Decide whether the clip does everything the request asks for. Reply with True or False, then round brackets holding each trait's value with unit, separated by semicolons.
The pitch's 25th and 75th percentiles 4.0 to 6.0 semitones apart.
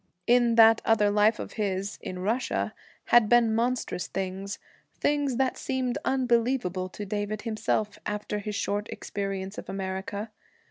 False (3.3 semitones)